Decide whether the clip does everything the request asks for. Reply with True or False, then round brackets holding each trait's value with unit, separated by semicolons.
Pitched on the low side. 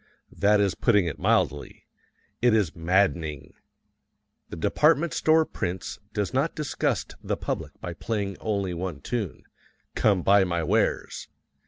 True (100 Hz)